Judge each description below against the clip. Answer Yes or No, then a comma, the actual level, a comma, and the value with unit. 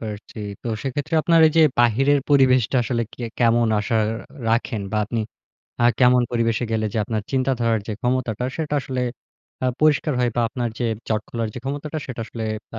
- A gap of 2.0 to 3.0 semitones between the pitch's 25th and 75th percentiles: Yes, average, 2.7 semitones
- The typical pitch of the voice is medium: No, low, 120 Hz